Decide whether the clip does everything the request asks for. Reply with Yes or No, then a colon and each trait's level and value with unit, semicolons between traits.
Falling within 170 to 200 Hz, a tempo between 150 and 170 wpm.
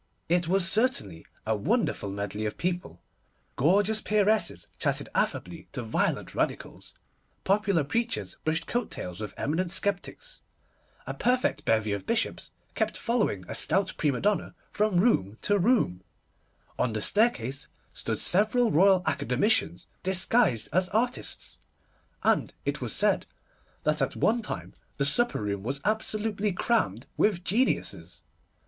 No: medium, 185 Hz; slow, 135 wpm